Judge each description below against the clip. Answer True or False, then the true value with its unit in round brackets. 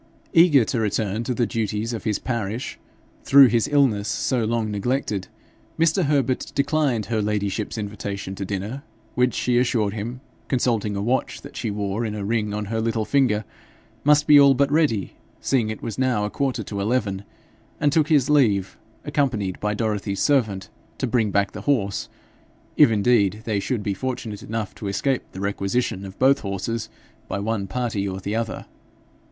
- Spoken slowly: False (175 wpm)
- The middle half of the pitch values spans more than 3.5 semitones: True (4.2 semitones)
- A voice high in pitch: False (110 Hz)